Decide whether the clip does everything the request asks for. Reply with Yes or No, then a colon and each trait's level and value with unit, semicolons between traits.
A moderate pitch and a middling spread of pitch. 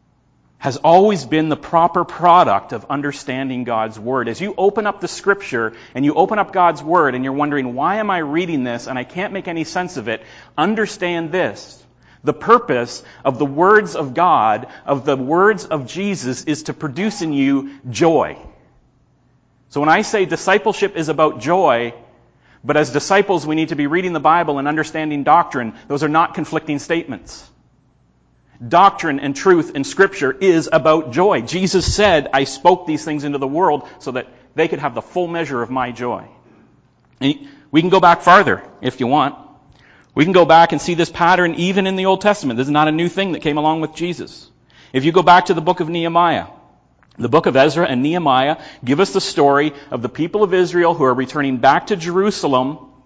Yes: medium, 155 Hz; average, 4.8 semitones